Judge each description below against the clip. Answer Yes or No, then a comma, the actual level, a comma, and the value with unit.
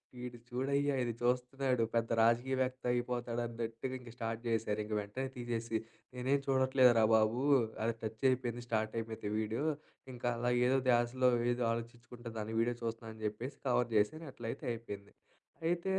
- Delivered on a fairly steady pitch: Yes, narrow, 2.0 semitones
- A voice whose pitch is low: Yes, low, 120 Hz